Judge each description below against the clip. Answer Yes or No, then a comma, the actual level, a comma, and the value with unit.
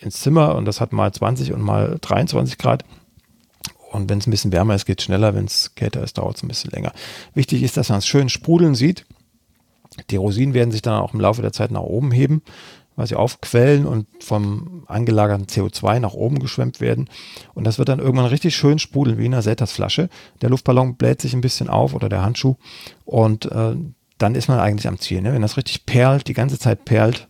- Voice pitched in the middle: No, low, 120 Hz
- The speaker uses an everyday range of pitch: Yes, average, 4.0 semitones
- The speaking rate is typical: No, fast, 225 wpm